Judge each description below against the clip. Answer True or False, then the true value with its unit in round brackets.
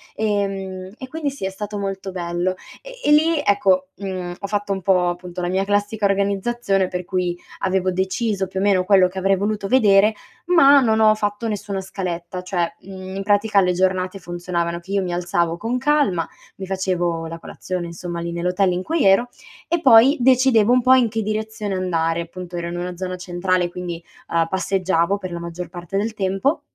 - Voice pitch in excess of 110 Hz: True (190 Hz)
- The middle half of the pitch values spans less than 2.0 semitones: False (2.7 semitones)